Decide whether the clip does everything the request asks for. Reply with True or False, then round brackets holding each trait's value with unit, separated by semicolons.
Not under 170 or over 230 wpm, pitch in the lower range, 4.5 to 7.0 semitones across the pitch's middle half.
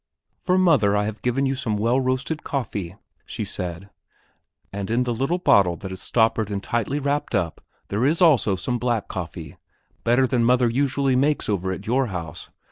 True (185 wpm; 115 Hz; 5.1 semitones)